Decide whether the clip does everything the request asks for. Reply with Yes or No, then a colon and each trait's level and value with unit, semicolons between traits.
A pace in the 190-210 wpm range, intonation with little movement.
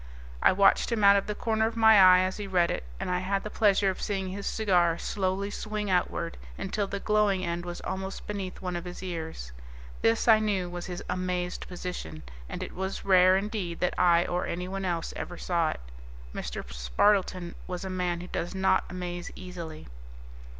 Yes: average, 195 wpm; narrow, 2.1 semitones